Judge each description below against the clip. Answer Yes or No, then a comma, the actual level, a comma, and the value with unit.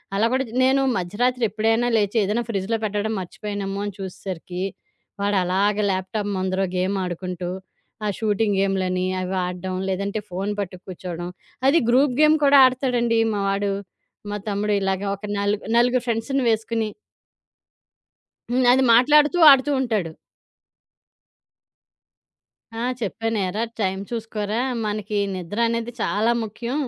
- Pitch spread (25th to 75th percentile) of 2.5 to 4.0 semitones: Yes, average, 3.5 semitones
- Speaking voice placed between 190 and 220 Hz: Yes, high, 210 Hz